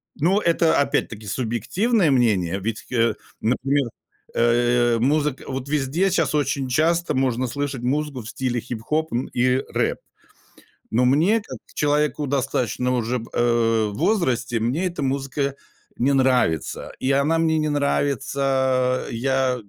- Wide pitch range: No, average, 3.5 semitones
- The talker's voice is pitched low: Yes, low, 130 Hz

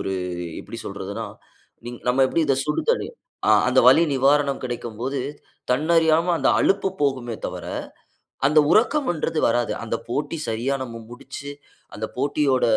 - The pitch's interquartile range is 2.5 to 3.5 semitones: No, average, 4.3 semitones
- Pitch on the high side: No, medium, 140 Hz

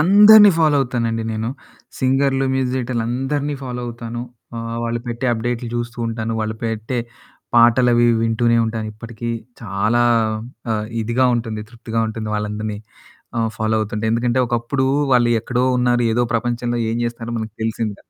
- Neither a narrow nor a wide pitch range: No, narrow, 1.6 semitones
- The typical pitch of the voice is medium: No, low, 120 Hz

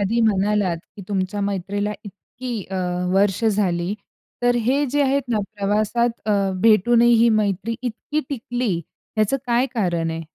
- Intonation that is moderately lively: Yes, average, 3.4 semitones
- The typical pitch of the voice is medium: No, high, 210 Hz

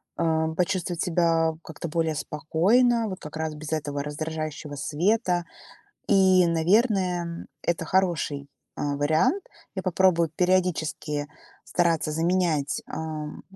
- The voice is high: No, medium, 165 Hz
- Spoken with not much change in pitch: No, average, 3.0 semitones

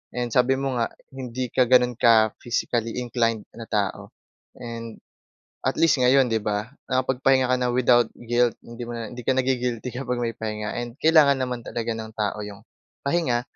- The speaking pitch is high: No, low, 120 Hz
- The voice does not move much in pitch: Yes, narrow, 1.8 semitones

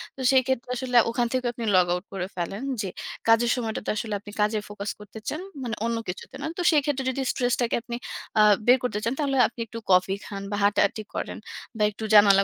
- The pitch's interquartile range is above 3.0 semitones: Yes, average, 3.5 semitones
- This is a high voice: Yes, high, 230 Hz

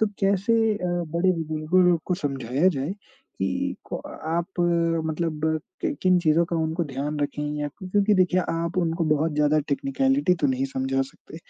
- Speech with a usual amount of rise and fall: Yes, average, 3.7 semitones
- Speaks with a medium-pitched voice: Yes, medium, 165 Hz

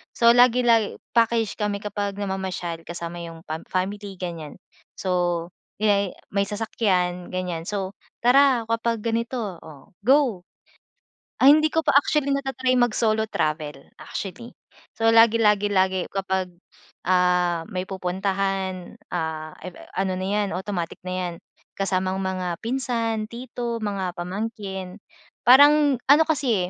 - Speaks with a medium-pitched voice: No, high, 200 Hz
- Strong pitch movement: No, average, 4.2 semitones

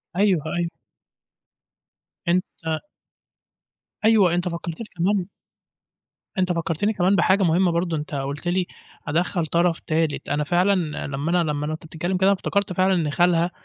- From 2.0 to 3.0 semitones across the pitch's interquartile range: Yes, narrow, 2.6 semitones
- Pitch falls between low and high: Yes, medium, 175 Hz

